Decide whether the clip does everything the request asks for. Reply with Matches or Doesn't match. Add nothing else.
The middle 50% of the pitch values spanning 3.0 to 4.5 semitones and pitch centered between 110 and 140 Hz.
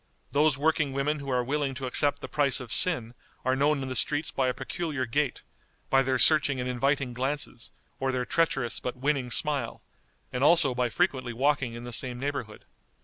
Doesn't match